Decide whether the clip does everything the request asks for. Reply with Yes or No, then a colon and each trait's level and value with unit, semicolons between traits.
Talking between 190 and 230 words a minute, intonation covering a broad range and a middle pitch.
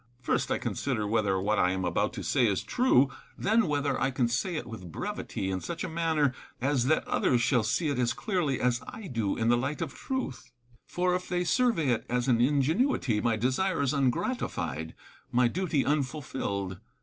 No: average, 195 wpm; wide, 6.0 semitones; low, 130 Hz